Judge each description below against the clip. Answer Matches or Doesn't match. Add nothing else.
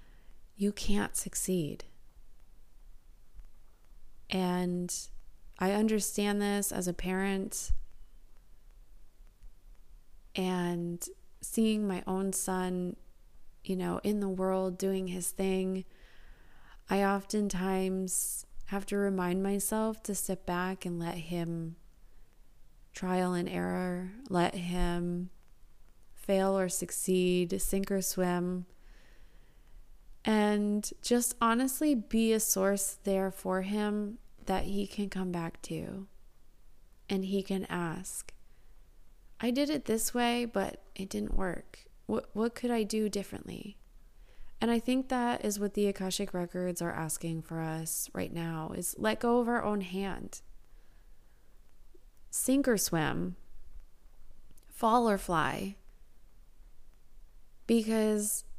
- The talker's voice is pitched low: Doesn't match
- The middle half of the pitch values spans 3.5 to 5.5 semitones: Doesn't match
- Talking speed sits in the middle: Doesn't match